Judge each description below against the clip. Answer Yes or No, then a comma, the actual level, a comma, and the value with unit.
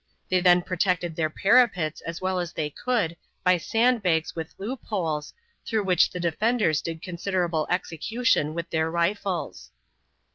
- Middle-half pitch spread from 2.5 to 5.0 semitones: Yes, average, 3.5 semitones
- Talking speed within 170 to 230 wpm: No, average, 150 wpm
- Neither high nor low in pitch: Yes, medium, 180 Hz